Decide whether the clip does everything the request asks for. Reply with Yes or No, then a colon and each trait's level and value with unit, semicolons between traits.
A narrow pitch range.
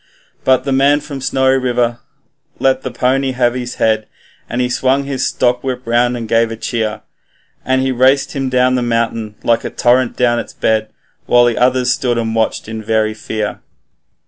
Yes: narrow, 2.1 semitones